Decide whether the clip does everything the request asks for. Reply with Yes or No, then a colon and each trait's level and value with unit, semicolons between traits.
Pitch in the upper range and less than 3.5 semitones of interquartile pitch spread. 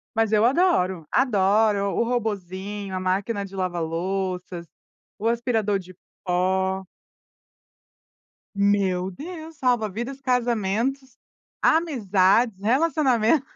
No: high, 205 Hz; average, 4.6 semitones